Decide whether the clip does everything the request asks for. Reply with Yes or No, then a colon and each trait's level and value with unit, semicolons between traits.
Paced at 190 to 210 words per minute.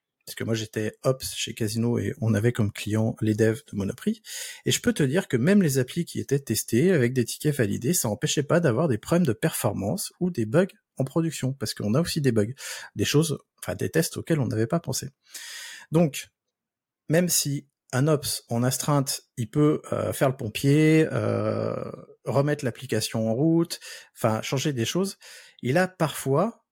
Yes: average, 195 wpm